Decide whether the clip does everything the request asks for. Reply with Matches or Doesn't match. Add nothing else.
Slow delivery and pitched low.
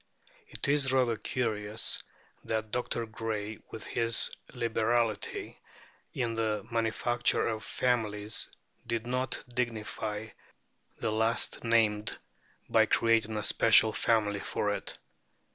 Matches